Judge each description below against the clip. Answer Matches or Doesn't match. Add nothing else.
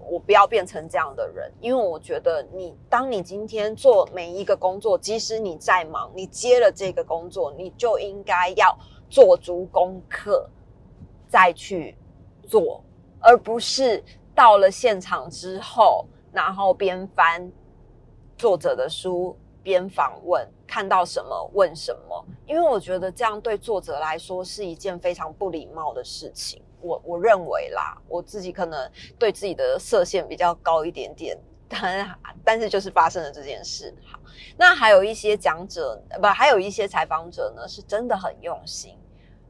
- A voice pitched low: Doesn't match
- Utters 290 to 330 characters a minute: Doesn't match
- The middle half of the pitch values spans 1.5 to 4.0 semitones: Doesn't match